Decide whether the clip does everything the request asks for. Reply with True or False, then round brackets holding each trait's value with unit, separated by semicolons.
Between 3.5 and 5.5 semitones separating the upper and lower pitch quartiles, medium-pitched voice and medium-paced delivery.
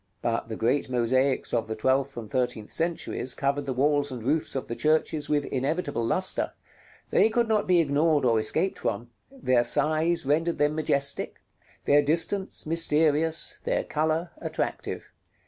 True (4.0 semitones; 145 Hz; 155 wpm)